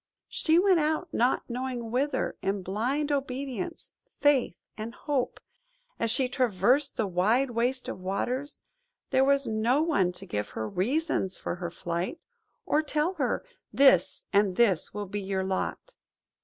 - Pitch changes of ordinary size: No, wide, 6.5 semitones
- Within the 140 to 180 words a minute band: Yes, average, 145 wpm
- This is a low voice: No, high, 245 Hz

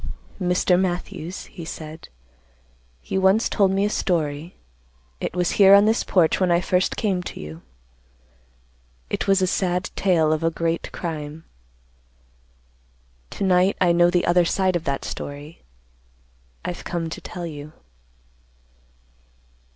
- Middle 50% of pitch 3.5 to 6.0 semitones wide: No, average, 2.7 semitones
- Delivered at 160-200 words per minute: No, average, 140 wpm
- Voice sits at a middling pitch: Yes, medium, 175 Hz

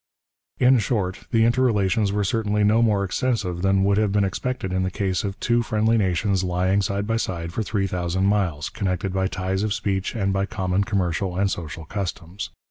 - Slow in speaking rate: No, average, 195 wpm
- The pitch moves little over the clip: Yes, narrow, 2.3 semitones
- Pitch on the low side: Yes, low, 100 Hz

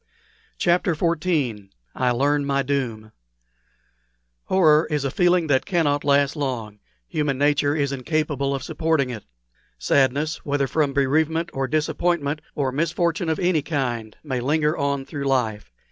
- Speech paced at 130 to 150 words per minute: Yes, average, 140 wpm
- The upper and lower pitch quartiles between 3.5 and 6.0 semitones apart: No, average, 2.8 semitones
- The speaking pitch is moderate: Yes, medium, 145 Hz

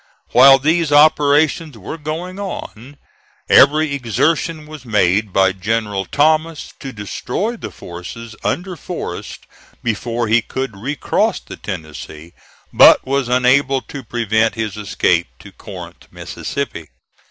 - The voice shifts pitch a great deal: Yes, wide, 6.0 semitones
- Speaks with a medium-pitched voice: No, low, 130 Hz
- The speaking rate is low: Yes, slow, 120 wpm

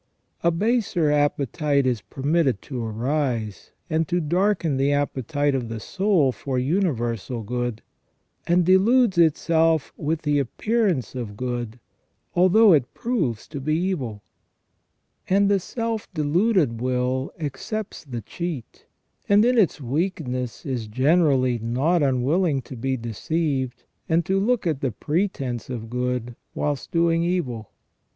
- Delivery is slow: Yes, slow, 130 wpm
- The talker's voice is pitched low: No, medium, 145 Hz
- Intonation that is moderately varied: No, wide, 5.7 semitones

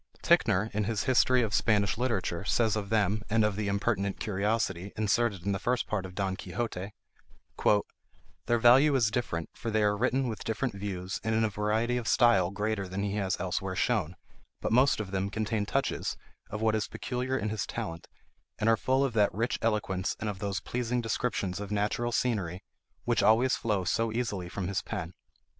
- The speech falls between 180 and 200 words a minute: Yes, average, 190 wpm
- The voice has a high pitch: No, low, 105 Hz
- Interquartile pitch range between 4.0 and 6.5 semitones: No, average, 2.9 semitones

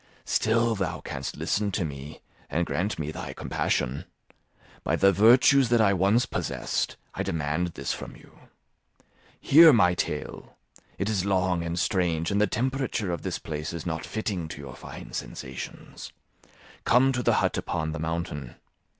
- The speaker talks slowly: No, average, 160 wpm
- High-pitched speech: No, very low, 90 Hz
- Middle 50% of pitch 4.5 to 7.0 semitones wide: Yes, wide, 5.4 semitones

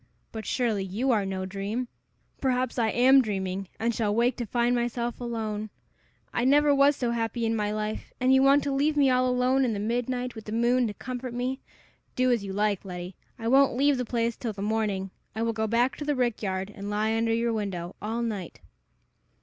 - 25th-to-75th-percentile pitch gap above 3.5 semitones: No, average, 3.1 semitones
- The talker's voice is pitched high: Yes, high, 230 Hz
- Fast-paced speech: Yes, fast, 215 wpm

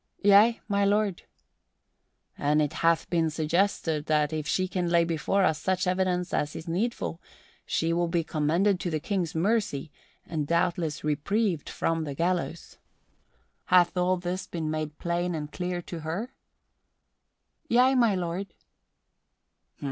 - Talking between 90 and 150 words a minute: Yes, average, 140 wpm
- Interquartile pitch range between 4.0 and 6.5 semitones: No, average, 3.0 semitones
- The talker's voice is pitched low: No, medium, 175 Hz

